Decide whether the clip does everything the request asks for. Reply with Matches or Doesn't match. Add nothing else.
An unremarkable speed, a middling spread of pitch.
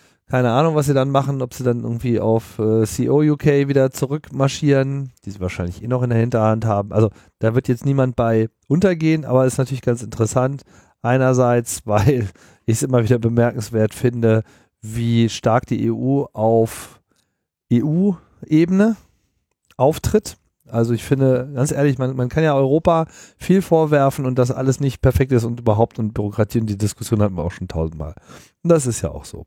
Matches